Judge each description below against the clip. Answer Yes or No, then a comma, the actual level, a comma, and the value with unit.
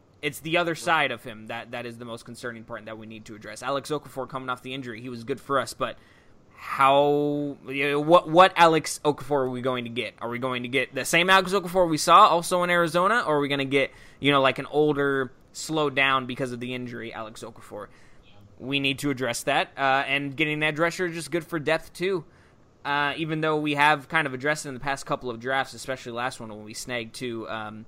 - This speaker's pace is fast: Yes, fast, 245 wpm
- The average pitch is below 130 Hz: No, low, 135 Hz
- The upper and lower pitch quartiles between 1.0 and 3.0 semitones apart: No, average, 3.8 semitones